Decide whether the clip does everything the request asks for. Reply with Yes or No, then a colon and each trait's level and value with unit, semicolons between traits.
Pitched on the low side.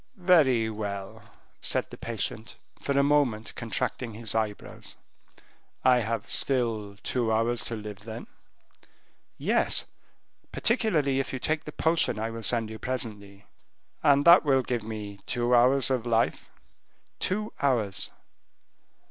Yes: low, 120 Hz